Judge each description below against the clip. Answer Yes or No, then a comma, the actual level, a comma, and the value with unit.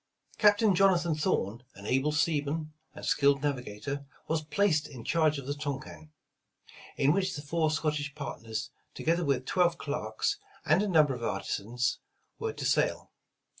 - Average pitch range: Yes, average, 3.6 semitones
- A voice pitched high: No, medium, 150 Hz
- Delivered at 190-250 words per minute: No, average, 150 wpm